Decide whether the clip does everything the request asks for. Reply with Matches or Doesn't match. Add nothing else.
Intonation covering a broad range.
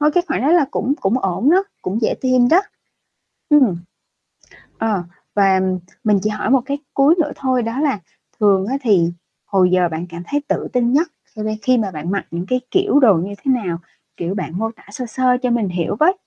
Matches